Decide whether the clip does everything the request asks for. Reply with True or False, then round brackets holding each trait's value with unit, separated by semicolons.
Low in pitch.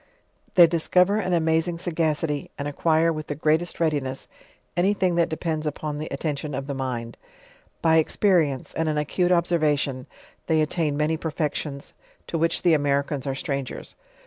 False (155 Hz)